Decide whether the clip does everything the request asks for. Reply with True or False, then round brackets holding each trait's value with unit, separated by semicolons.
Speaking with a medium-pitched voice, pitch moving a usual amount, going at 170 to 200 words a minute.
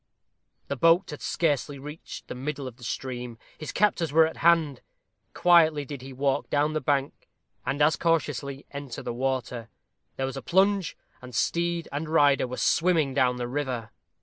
True (145 Hz; 3.6 semitones; 175 wpm)